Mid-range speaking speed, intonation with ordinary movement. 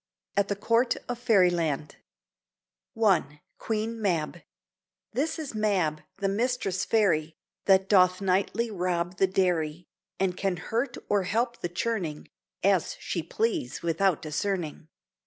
No: slow, 125 wpm; average, 4.0 semitones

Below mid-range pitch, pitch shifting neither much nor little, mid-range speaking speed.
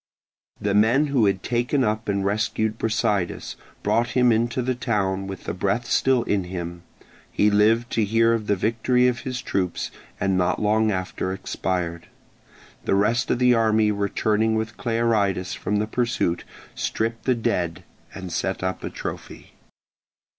Yes: low, 110 Hz; average, 3.3 semitones; average, 160 wpm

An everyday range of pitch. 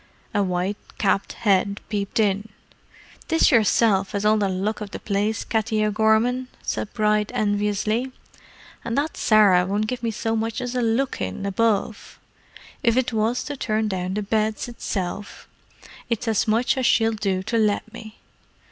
No: narrow, 2.2 semitones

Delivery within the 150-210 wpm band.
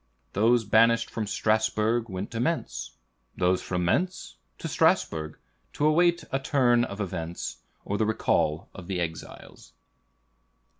No: slow, 135 wpm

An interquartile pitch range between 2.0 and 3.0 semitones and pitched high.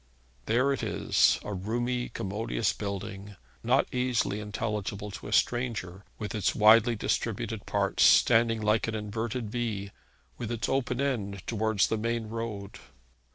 No: narrow, 2.6 semitones; low, 110 Hz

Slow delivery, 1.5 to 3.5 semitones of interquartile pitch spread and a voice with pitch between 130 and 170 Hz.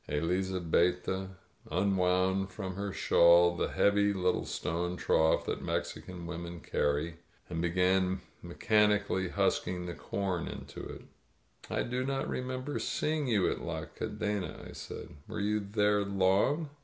No: slow, 130 wpm; average, 2.9 semitones; very low, 95 Hz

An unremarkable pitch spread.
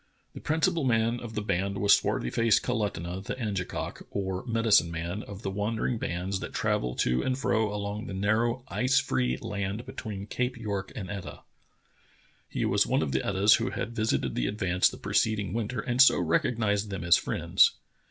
Yes: average, 3.2 semitones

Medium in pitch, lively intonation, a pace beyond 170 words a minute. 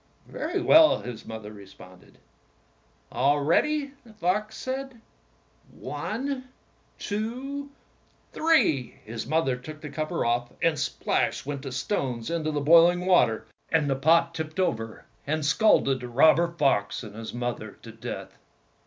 No: medium, 155 Hz; wide, 8.9 semitones; slow, 135 wpm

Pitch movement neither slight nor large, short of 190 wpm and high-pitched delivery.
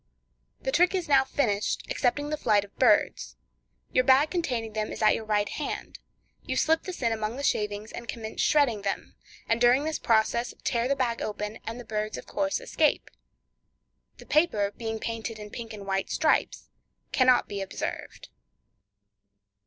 Yes: average, 4.7 semitones; average, 170 wpm; high, 235 Hz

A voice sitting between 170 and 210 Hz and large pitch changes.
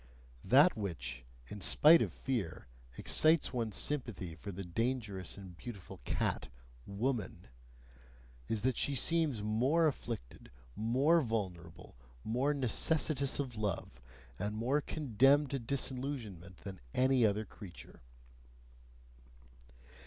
No: low, 115 Hz; wide, 5.7 semitones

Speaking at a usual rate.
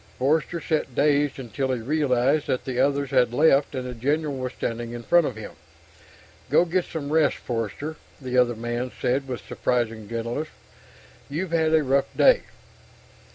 Yes: average, 165 wpm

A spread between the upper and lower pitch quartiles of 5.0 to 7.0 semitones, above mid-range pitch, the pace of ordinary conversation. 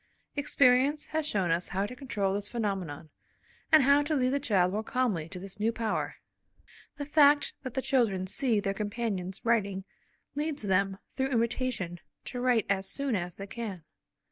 Yes: wide, 5.4 semitones; high, 225 Hz; average, 170 wpm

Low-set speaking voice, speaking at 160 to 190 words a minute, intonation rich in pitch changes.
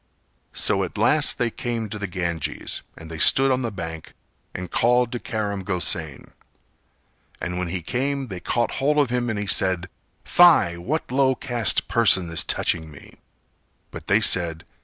Yes: low, 100 Hz; average, 170 wpm; wide, 6.2 semitones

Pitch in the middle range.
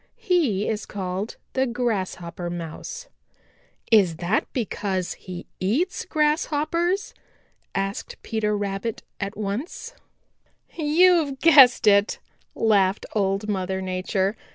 No: high, 210 Hz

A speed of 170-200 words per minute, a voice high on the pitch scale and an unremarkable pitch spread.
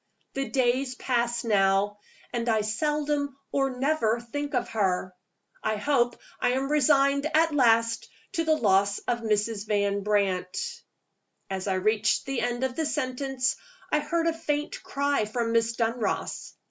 No: average, 150 wpm; high, 245 Hz; average, 4.9 semitones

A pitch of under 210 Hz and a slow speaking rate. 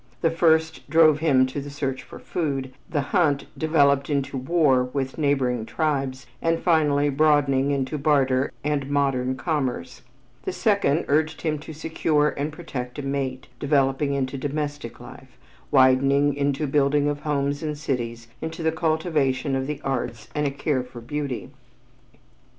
No: medium, 140 Hz; average, 155 wpm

